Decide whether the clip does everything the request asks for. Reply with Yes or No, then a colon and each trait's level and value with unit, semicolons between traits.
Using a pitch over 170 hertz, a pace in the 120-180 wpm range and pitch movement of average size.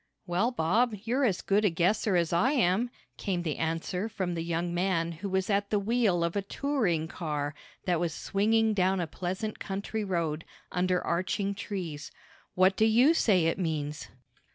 Yes: medium, 185 Hz; average, 175 wpm; average, 3.8 semitones